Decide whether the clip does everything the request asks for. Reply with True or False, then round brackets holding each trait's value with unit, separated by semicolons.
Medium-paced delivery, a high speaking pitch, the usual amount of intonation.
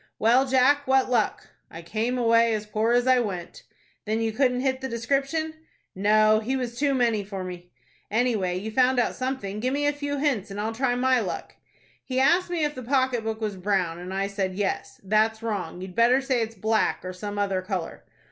False (210 wpm; 225 Hz; 4.2 semitones)